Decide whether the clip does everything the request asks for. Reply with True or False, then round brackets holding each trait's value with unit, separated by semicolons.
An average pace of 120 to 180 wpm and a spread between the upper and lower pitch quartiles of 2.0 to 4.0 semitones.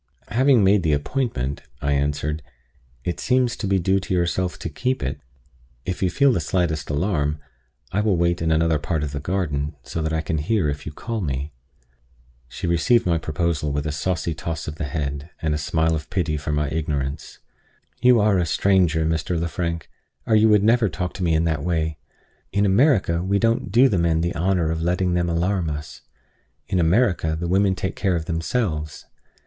False (200 wpm; 3.7 semitones)